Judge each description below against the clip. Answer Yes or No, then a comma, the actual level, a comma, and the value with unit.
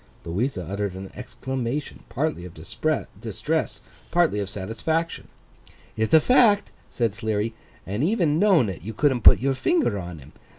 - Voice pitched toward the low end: Yes, low, 115 Hz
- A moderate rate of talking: Yes, average, 145 wpm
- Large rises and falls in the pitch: Yes, wide, 7.8 semitones